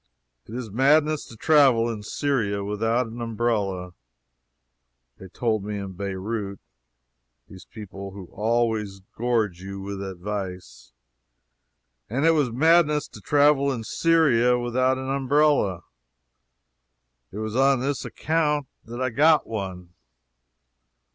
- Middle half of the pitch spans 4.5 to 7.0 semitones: Yes, wide, 5.5 semitones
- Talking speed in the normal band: No, slow, 120 wpm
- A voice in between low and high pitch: No, low, 115 Hz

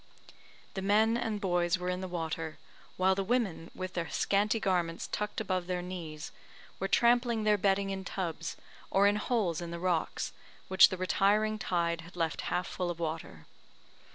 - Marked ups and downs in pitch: No, average, 3.1 semitones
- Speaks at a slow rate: No, average, 175 wpm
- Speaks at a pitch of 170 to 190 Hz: Yes, medium, 185 Hz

